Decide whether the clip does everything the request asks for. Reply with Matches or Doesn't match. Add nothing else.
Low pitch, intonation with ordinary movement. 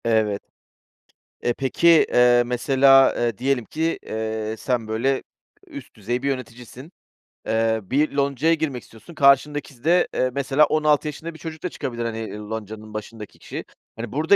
Matches